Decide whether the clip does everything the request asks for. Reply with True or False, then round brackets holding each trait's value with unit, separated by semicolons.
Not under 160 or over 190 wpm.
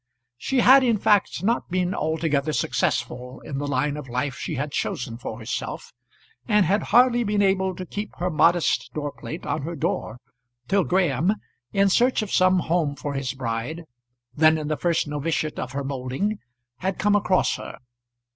True (175 wpm)